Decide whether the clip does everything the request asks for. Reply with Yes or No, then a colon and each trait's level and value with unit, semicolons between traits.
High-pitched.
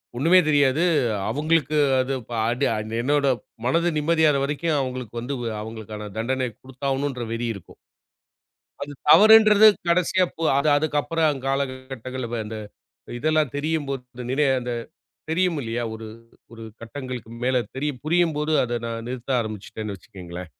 No: low, 135 Hz